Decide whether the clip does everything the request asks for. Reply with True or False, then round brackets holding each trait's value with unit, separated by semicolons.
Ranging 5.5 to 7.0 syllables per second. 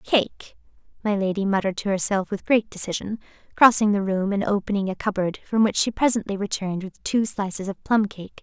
True (5.6 syllables/s)